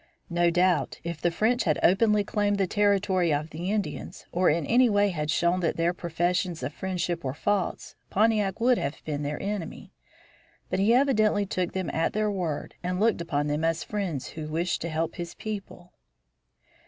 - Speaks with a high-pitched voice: No, medium, 180 Hz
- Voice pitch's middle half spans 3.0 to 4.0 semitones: Yes, average, 3.7 semitones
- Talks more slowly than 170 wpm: No, average, 185 wpm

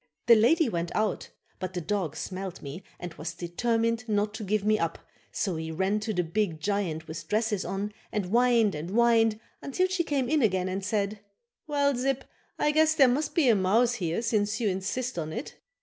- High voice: Yes, high, 210 Hz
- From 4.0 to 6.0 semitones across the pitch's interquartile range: Yes, average, 4.5 semitones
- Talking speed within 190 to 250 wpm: Yes, average, 200 wpm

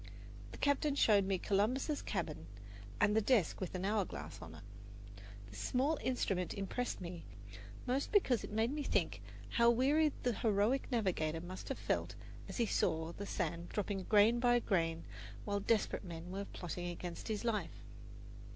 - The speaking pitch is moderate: No, high, 205 Hz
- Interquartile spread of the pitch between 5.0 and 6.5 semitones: Yes, wide, 5.5 semitones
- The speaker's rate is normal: Yes, average, 165 wpm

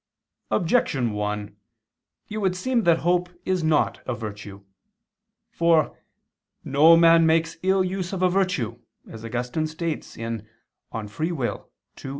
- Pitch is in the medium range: Yes, medium, 160 Hz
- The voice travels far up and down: Yes, wide, 7.7 semitones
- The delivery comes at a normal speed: No, slow, 130 wpm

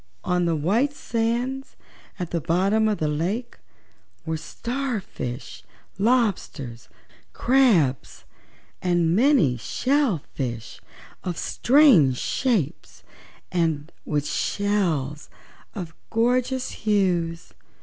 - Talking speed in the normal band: No, slow, 95 wpm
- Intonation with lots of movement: Yes, wide, 7.1 semitones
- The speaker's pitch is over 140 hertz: Yes, medium, 185 Hz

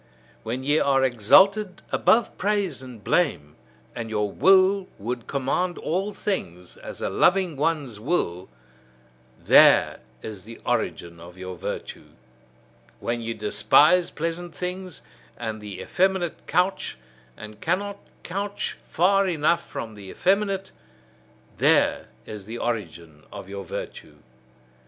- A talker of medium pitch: Yes, medium, 145 Hz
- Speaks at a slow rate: Yes, slow, 125 wpm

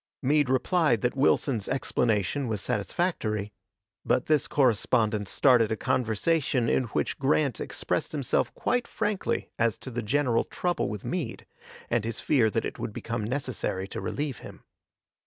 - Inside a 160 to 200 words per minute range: No, average, 150 wpm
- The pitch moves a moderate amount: Yes, average, 4.7 semitones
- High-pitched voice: No, low, 125 Hz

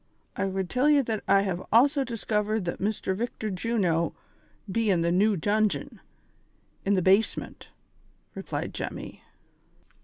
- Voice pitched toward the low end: No, high, 205 Hz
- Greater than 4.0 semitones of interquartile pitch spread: No, average, 3.1 semitones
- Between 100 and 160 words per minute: Yes, average, 150 wpm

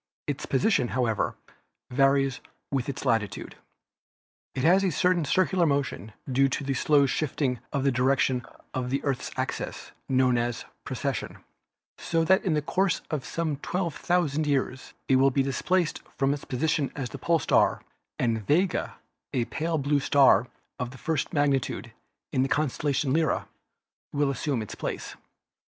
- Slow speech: No, average, 155 wpm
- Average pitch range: Yes, average, 3.2 semitones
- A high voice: No, medium, 140 Hz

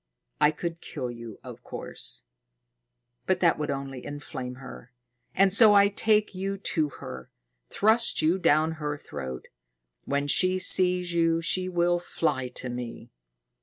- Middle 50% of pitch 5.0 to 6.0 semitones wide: Yes, wide, 5.6 semitones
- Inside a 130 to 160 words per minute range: Yes, average, 145 wpm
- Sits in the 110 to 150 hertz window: No, medium, 160 Hz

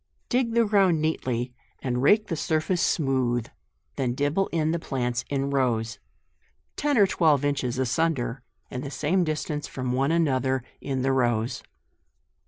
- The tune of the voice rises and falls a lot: No, average, 4.4 semitones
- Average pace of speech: Yes, average, 165 wpm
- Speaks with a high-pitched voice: No, medium, 140 Hz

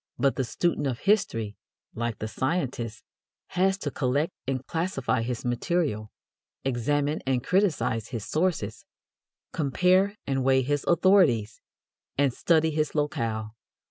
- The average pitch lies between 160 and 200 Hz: No, low, 135 Hz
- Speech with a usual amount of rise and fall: No, wide, 6.0 semitones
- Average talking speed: No, slow, 125 wpm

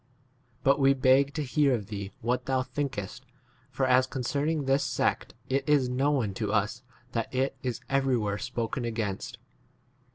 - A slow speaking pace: No, average, 165 wpm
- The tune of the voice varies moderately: Yes, average, 3.0 semitones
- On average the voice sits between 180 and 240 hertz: No, low, 130 Hz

